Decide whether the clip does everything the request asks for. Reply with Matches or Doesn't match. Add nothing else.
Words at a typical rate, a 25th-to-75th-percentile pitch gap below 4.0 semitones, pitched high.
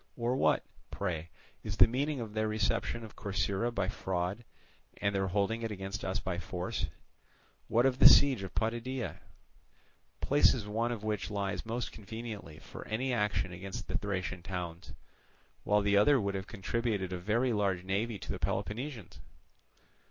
Doesn't match